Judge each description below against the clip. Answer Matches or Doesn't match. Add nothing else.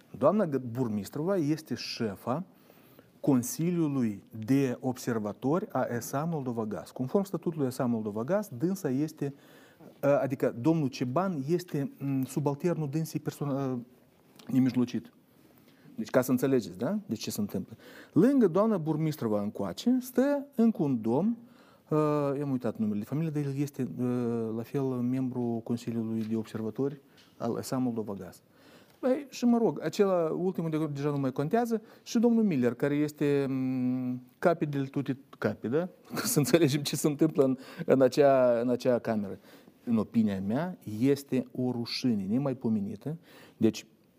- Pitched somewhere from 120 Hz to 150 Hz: Matches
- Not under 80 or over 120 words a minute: Doesn't match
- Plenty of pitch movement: Matches